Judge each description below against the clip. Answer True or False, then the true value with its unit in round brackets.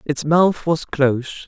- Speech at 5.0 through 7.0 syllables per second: False (4.0 syllables/s)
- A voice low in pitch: False (150 Hz)